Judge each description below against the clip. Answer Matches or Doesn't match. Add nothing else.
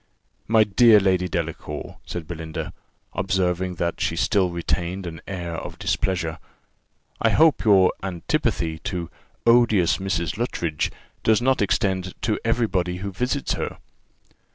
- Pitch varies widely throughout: Doesn't match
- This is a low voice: Matches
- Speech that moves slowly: Matches